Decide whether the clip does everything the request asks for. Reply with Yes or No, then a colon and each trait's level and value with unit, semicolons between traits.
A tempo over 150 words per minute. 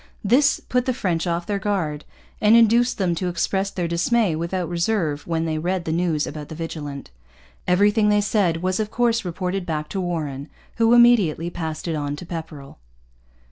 Yes: average, 180 wpm